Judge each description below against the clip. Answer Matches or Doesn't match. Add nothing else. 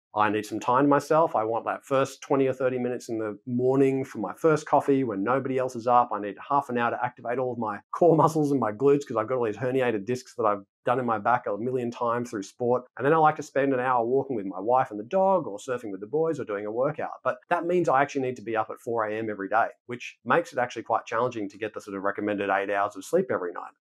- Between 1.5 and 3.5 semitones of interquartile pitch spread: Doesn't match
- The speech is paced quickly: Matches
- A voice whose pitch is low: Matches